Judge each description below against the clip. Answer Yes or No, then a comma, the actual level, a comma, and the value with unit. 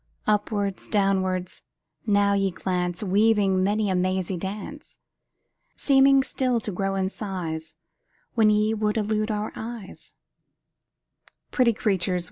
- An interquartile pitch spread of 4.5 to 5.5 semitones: No, narrow, 2.5 semitones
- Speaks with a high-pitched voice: Yes, high, 205 Hz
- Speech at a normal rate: No, slow, 115 wpm